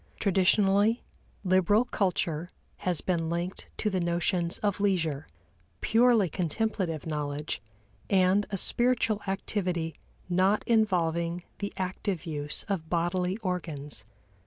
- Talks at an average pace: No, slow, 110 wpm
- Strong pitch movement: No, average, 3.3 semitones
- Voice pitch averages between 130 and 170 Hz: No, medium, 185 Hz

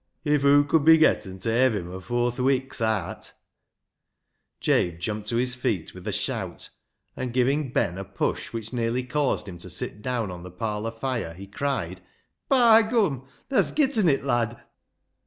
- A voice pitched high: No, low, 120 Hz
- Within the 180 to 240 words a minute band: Yes, average, 185 wpm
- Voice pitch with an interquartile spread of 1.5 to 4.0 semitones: No, average, 5.1 semitones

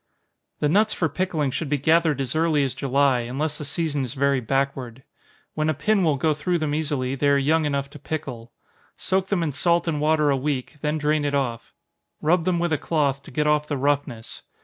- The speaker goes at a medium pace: No, fast, 220 wpm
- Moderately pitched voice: Yes, medium, 150 Hz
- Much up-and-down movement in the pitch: No, narrow, 2.5 semitones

